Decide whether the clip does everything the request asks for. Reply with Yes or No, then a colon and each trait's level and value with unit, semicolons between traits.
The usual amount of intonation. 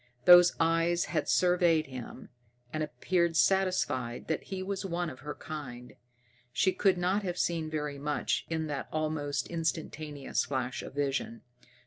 Yes: average, 3.5 semitones